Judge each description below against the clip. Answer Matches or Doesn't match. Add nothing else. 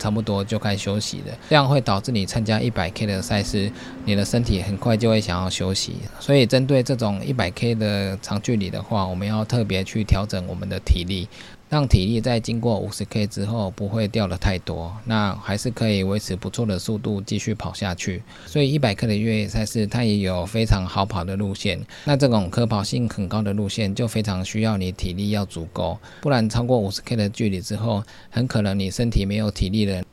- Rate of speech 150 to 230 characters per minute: Doesn't match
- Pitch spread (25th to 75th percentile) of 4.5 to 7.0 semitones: Doesn't match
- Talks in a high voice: Doesn't match